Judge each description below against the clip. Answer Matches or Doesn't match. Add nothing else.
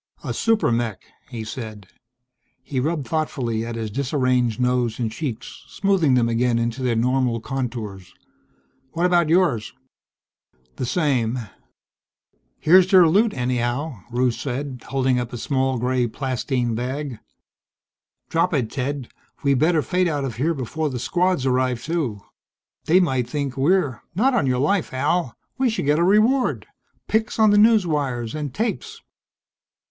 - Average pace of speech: Matches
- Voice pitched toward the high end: Doesn't match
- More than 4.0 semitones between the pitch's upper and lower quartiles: Matches